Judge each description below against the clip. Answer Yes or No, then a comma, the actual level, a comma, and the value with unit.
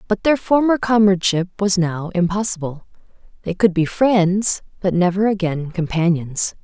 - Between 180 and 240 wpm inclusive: No, slow, 135 wpm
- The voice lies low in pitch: No, high, 190 Hz